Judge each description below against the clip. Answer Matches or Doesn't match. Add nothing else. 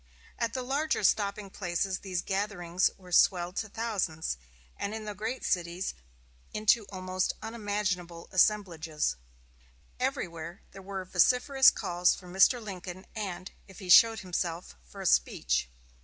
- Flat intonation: Doesn't match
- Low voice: Doesn't match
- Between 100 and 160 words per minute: Matches